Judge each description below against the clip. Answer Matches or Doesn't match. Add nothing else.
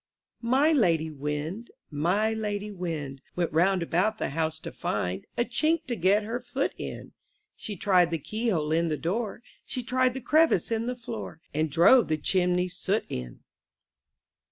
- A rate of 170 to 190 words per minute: Matches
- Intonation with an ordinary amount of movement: Doesn't match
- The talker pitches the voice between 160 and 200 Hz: Matches